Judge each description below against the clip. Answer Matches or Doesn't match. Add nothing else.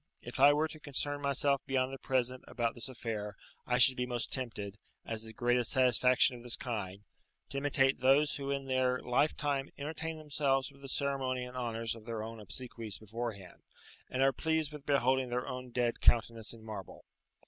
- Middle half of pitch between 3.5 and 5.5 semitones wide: Doesn't match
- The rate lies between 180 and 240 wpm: Matches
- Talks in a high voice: Doesn't match